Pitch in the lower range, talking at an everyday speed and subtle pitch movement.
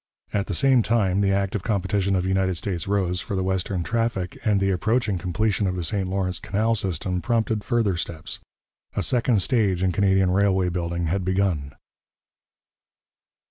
Yes: very low, 95 Hz; average, 165 wpm; narrow, 2.3 semitones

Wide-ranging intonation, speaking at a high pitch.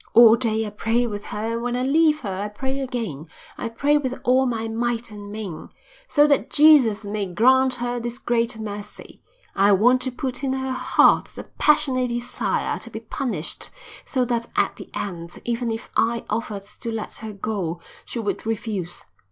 No: average, 3.4 semitones; high, 230 Hz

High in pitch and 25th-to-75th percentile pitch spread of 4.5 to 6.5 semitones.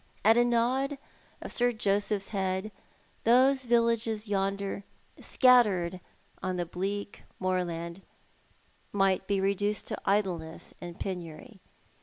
No: high, 200 Hz; average, 3.8 semitones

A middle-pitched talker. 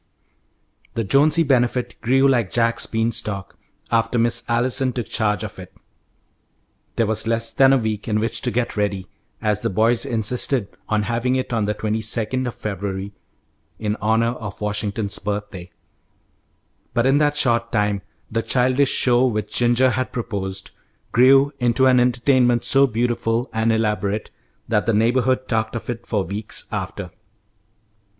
No: low, 115 Hz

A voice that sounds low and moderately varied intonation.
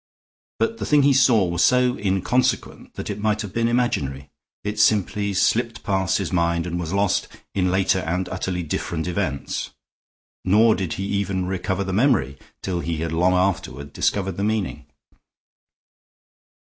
Yes: very low, 95 Hz; average, 3.5 semitones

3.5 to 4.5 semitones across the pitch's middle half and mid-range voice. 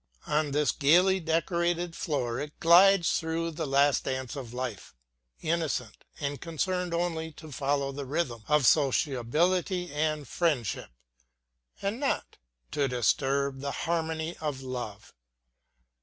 Yes: average, 3.8 semitones; medium, 150 Hz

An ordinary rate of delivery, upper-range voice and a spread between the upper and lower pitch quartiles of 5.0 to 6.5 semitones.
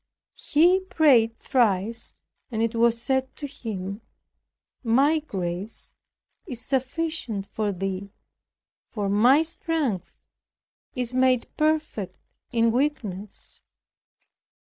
No: slow, 95 wpm; high, 235 Hz; wide, 5.6 semitones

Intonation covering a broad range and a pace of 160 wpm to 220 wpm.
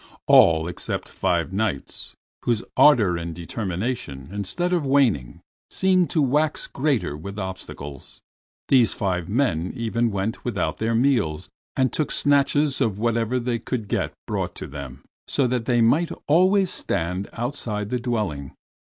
No: wide, 6.7 semitones; average, 145 wpm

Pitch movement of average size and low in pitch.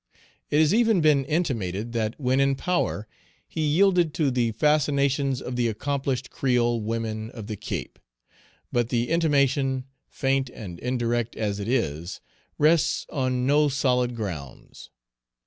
Yes: average, 4.0 semitones; low, 130 Hz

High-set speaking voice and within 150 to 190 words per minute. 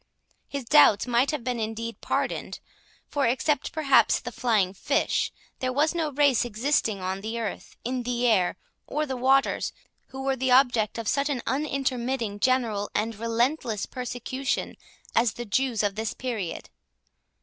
Yes: high, 245 Hz; average, 155 wpm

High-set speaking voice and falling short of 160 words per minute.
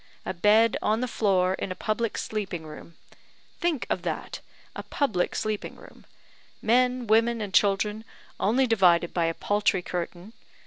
Yes: high, 210 Hz; average, 150 wpm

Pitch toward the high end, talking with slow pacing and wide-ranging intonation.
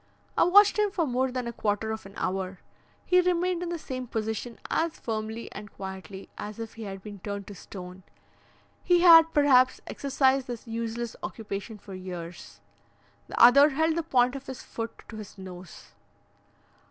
No: high, 230 Hz; average, 175 wpm; wide, 5.8 semitones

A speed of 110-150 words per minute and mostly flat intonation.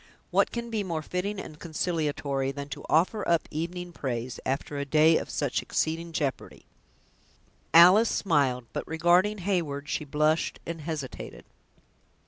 No: average, 140 wpm; average, 3.6 semitones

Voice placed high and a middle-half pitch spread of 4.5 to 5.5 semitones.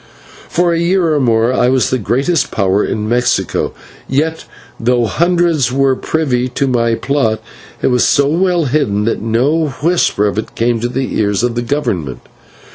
No: low, 125 Hz; average, 5.0 semitones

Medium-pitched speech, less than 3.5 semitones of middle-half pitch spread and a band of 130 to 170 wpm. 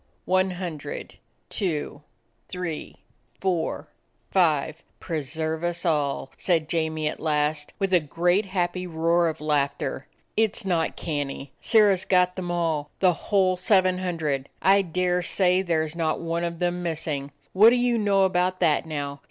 Yes: medium, 170 Hz; average, 3.0 semitones; average, 160 wpm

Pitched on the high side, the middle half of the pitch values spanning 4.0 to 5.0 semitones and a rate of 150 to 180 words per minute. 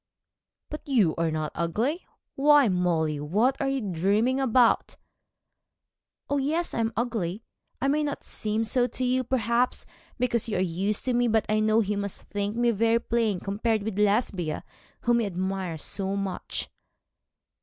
Yes: high, 220 Hz; average, 4.3 semitones; average, 165 wpm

